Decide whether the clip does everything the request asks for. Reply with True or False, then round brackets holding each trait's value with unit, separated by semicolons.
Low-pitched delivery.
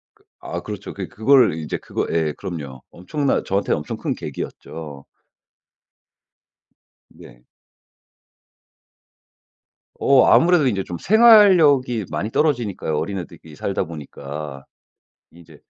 True (95 Hz)